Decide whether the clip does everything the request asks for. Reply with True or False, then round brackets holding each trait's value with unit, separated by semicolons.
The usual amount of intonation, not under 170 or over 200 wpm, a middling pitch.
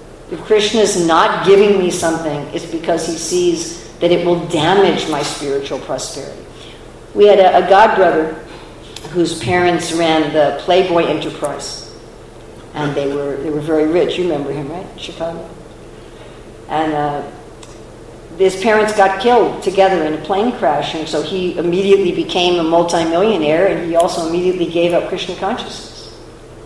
False (3.8 semitones; 150 wpm; 170 Hz)